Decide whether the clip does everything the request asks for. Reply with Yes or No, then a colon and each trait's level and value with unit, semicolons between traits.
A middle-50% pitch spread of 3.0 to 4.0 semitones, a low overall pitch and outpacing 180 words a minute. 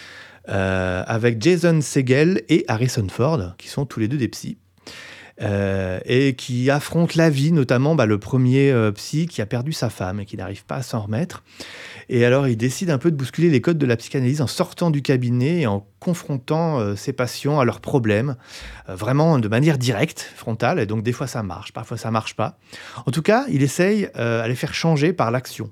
No: wide, 5.5 semitones; low, 130 Hz; average, 215 wpm